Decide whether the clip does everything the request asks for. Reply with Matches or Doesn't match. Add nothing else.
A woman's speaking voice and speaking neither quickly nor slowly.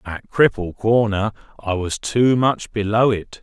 Doesn't match